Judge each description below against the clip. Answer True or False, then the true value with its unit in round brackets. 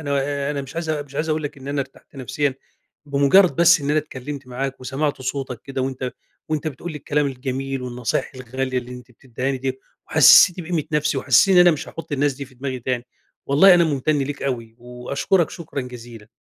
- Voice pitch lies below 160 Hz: True (140 Hz)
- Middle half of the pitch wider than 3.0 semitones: False (2.6 semitones)